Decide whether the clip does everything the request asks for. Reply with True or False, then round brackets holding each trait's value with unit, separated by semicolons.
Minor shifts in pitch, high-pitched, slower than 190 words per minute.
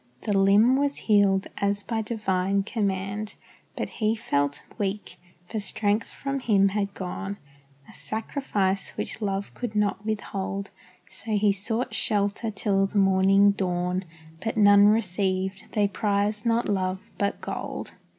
True (1.8 semitones; 200 Hz; 140 wpm)